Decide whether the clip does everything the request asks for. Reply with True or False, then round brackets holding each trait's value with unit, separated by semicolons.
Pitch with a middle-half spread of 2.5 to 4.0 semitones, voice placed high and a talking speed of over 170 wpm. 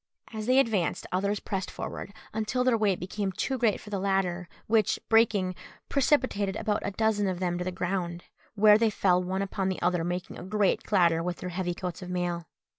True (2.9 semitones; 195 Hz; 200 wpm)